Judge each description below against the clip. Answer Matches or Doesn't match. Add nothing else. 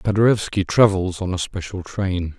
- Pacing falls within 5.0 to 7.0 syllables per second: Doesn't match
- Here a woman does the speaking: Doesn't match